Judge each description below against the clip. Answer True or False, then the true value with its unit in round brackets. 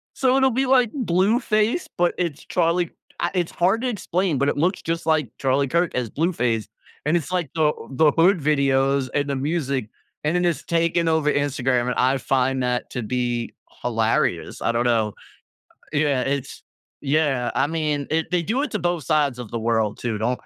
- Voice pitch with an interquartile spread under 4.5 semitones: False (5.1 semitones)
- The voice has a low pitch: False (150 Hz)